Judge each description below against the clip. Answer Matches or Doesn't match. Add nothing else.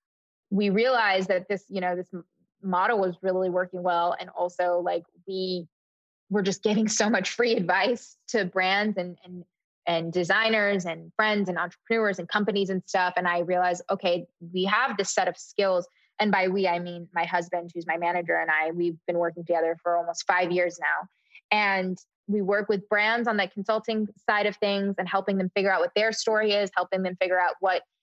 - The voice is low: Doesn't match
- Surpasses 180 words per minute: Matches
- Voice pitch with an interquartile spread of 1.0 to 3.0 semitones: Matches